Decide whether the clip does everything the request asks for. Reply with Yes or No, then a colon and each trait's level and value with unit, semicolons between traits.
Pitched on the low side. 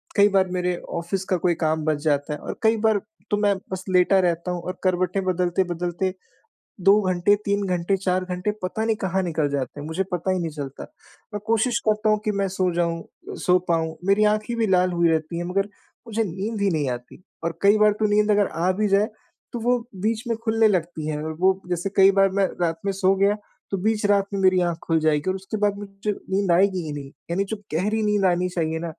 No: medium, 185 Hz